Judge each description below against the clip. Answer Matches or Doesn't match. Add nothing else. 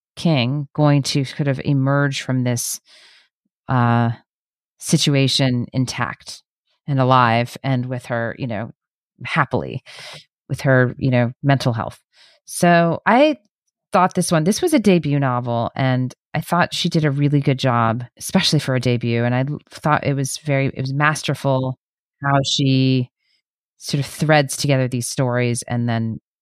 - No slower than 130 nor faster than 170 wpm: Matches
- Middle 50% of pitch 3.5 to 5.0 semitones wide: Doesn't match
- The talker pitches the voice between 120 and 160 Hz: Matches